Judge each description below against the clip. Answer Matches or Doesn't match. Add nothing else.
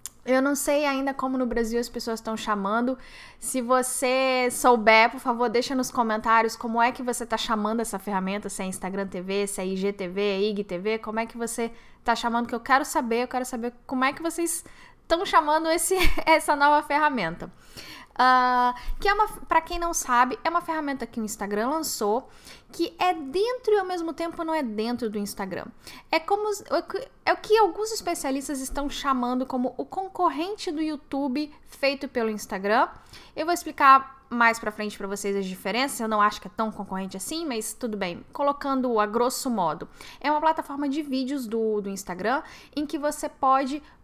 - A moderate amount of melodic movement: Doesn't match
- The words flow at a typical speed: Doesn't match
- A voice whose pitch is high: Matches